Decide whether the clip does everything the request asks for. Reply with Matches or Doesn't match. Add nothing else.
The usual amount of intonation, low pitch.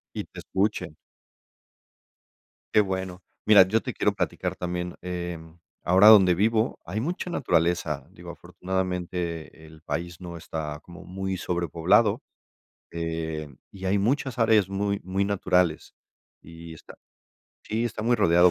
Matches